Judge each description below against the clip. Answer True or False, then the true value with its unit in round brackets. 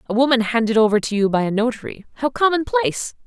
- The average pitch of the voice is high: True (235 Hz)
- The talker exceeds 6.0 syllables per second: True (6.6 syllables/s)